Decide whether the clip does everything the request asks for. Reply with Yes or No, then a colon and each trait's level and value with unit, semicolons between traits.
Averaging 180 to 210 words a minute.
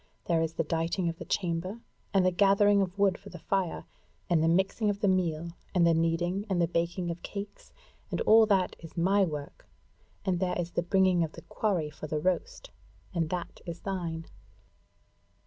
Yes: average, 195 wpm